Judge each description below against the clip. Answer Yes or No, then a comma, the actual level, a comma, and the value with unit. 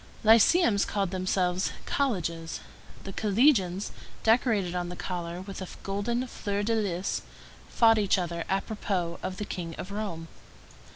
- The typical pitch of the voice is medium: No, high, 195 Hz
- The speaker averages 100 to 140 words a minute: Yes, slow, 135 wpm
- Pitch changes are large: No, average, 3.4 semitones